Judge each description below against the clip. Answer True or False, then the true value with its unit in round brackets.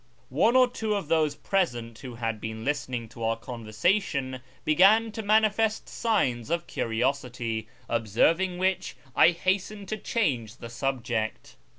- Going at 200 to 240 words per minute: False (145 wpm)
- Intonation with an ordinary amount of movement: False (8.9 semitones)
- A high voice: False (140 Hz)